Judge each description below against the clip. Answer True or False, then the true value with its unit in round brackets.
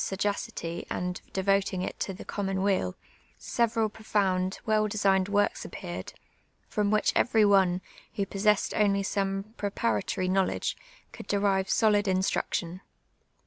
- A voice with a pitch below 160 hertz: False (195 Hz)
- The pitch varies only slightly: True (1.6 semitones)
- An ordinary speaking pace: False (125 wpm)